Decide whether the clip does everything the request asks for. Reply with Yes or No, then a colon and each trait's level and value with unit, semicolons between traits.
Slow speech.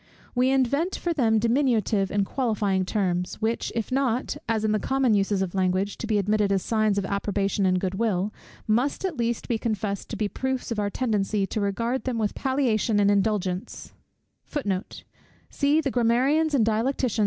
No: average, 160 wpm